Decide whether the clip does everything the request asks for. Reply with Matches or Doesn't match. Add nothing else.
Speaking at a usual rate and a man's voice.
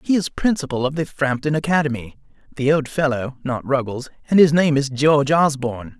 Matches